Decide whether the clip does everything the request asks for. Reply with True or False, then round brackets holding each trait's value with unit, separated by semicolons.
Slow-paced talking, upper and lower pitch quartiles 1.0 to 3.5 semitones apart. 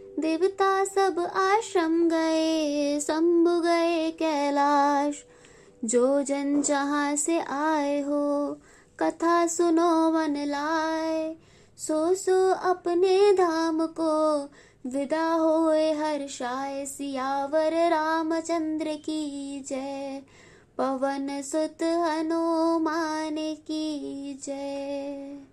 True (80 wpm; 2.7 semitones)